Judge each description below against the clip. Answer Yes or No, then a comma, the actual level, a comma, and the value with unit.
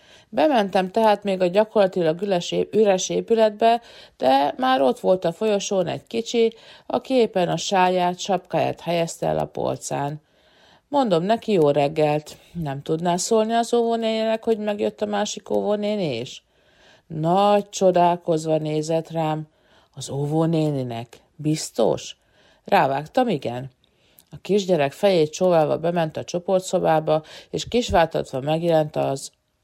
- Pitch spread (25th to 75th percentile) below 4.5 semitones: No, average, 5.2 semitones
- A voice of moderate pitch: Yes, medium, 180 Hz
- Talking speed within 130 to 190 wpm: No, average, 120 wpm